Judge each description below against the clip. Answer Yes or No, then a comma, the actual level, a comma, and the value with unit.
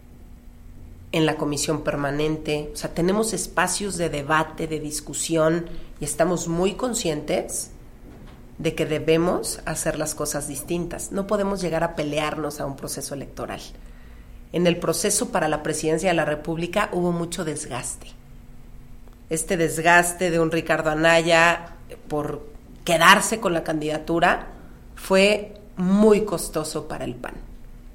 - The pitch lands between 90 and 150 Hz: No, medium, 160 Hz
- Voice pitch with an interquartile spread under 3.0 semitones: Yes, narrow, 2.6 semitones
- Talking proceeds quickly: No, average, 130 wpm